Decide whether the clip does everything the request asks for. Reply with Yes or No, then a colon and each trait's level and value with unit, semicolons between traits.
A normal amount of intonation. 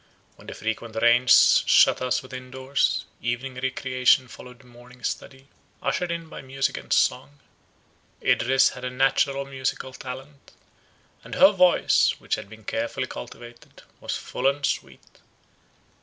No: narrow, 1.7 semitones